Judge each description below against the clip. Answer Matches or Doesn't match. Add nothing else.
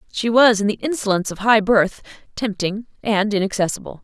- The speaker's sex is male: Doesn't match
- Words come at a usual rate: Matches